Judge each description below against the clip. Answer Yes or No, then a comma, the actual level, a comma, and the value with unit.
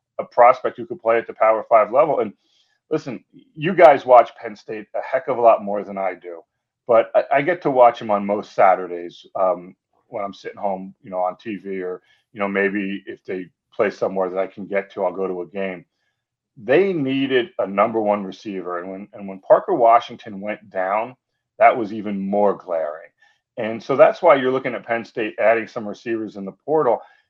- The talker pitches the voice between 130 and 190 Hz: No, low, 100 Hz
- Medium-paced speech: No, fast, 210 wpm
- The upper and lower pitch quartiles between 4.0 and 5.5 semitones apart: No, average, 3.3 semitones